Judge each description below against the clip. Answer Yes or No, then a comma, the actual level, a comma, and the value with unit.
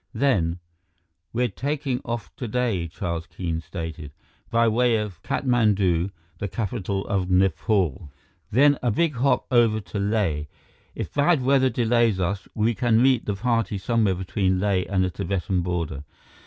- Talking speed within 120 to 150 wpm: Yes, average, 145 wpm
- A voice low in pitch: Yes, low, 105 Hz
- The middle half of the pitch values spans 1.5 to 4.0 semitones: No, average, 4.6 semitones